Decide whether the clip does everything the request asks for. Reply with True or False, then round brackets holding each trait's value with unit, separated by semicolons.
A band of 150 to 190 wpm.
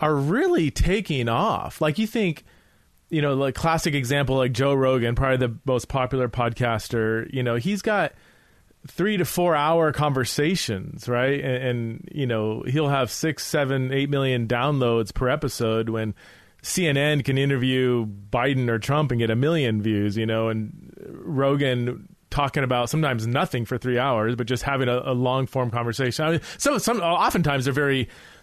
True (170 wpm)